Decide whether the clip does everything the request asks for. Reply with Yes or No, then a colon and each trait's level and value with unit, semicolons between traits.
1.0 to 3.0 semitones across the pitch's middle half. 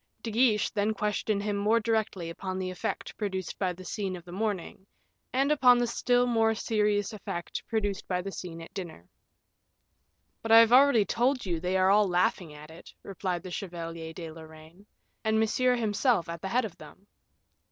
No: average, 4.0 semitones